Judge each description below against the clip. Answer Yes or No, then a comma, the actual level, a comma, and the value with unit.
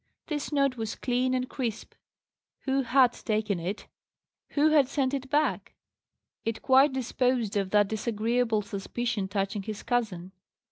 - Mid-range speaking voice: No, high, 240 Hz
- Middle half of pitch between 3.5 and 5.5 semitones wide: Yes, average, 3.9 semitones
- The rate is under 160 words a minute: Yes, average, 140 wpm